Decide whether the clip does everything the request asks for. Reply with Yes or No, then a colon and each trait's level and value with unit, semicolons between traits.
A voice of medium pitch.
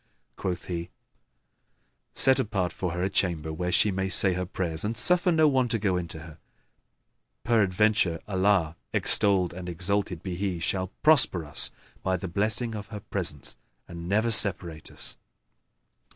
No: very low, 95 Hz